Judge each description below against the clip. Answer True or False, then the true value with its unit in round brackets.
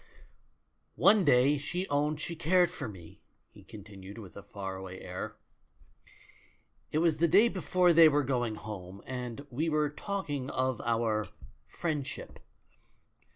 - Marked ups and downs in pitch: True (7.0 semitones)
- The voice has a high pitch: False (140 Hz)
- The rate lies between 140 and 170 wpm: True (145 wpm)